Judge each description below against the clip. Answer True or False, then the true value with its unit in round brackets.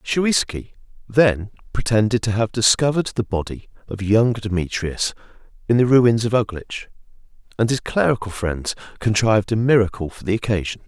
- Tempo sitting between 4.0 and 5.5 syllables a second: True (5.1 syllables/s)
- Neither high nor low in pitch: False (110 Hz)